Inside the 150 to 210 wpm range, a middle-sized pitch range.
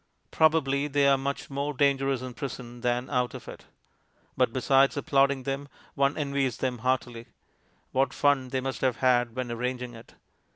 No: average, 165 wpm; narrow, 1.9 semitones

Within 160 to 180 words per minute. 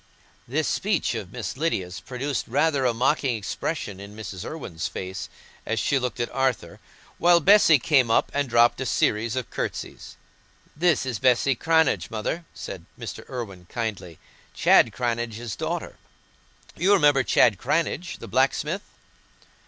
No: average, 145 wpm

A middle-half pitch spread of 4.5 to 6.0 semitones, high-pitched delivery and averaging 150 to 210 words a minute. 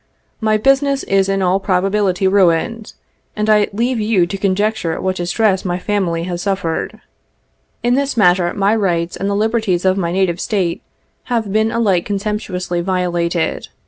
No: average, 3.2 semitones; high, 195 Hz; average, 155 wpm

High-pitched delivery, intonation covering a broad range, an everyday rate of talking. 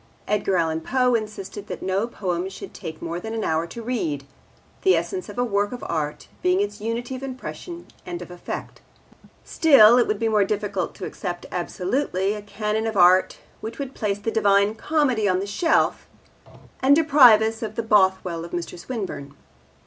No: high, 210 Hz; average, 4.3 semitones; average, 180 wpm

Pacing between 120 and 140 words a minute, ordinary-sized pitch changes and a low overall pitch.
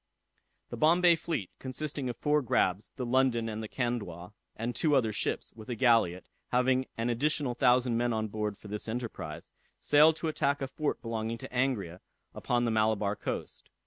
No: average, 175 wpm; average, 3.6 semitones; low, 120 Hz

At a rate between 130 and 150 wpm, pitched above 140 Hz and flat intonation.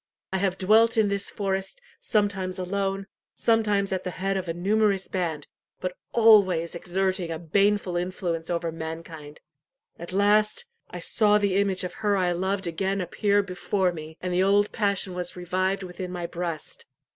No: average, 165 wpm; high, 190 Hz; narrow, 2.2 semitones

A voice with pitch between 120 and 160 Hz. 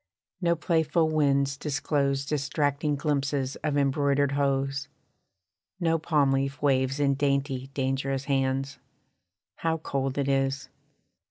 Yes: medium, 140 Hz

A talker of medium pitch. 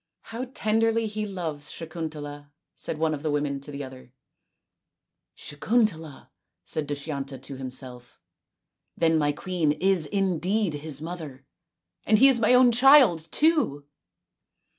Yes: medium, 160 Hz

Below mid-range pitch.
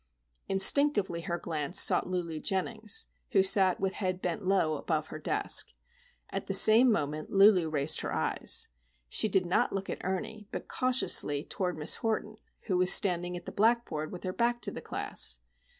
No: medium, 185 Hz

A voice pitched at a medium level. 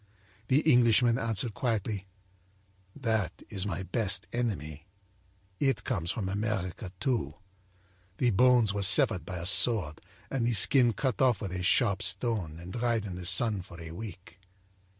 No: low, 105 Hz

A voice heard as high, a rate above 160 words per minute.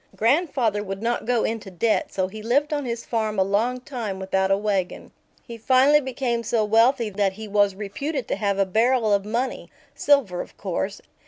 Yes: high, 220 Hz; average, 190 wpm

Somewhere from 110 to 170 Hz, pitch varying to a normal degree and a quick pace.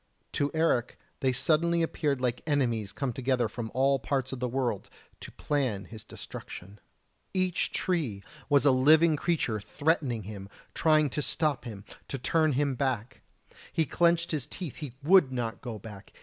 No: low, 135 Hz; average, 4.7 semitones; average, 165 wpm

